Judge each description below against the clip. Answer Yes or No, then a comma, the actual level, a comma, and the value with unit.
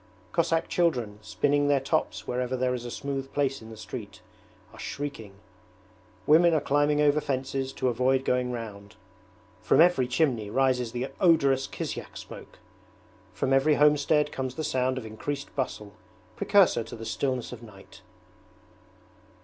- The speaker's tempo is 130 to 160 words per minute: Yes, average, 150 wpm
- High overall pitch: No, low, 130 Hz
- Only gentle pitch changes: No, average, 3.2 semitones